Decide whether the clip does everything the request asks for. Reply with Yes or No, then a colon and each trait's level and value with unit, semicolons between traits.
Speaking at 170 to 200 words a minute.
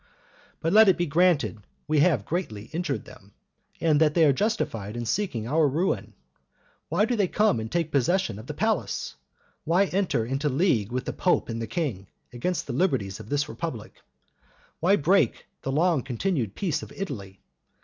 Yes: average, 180 wpm